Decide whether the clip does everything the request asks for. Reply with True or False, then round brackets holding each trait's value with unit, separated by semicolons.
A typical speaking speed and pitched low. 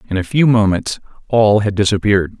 True (175 wpm; 105 Hz)